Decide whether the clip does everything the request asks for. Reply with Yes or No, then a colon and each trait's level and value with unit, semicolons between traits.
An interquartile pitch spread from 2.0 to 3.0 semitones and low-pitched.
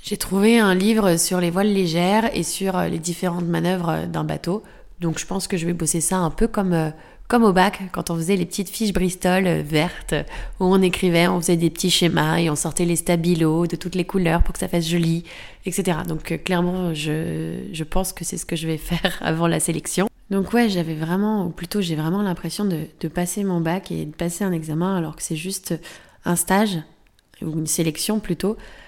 No: narrow, 2.4 semitones; medium, 175 Hz